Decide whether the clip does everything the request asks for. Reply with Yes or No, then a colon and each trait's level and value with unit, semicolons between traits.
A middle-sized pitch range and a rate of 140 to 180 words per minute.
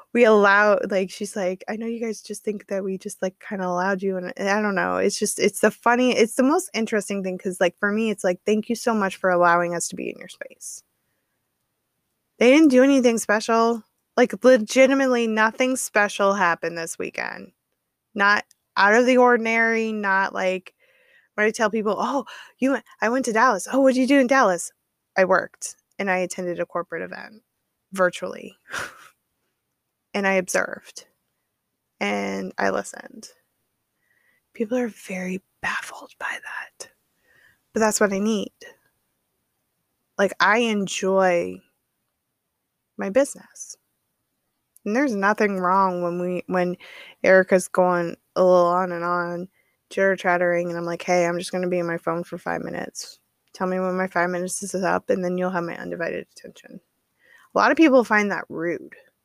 Yes: average, 3.9 semitones; average, 175 wpm